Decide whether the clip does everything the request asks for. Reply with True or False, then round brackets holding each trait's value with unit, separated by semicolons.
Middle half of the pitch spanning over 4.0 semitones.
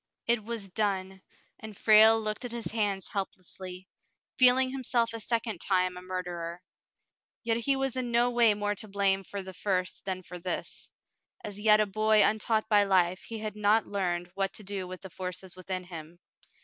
False (3.1 semitones)